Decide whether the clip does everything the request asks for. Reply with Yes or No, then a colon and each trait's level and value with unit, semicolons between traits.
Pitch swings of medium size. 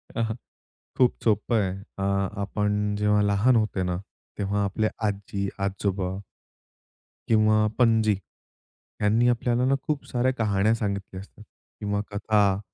No: narrow, 2.0 semitones